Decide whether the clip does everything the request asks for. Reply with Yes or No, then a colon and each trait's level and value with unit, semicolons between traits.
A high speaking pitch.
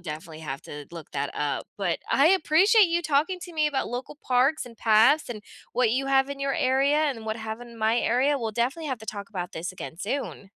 Yes: high, 245 Hz